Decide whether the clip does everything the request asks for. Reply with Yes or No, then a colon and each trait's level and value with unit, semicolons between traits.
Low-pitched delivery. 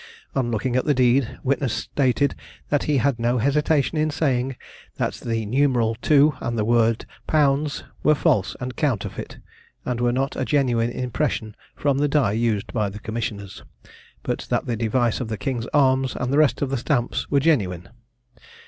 Yes: low, 125 Hz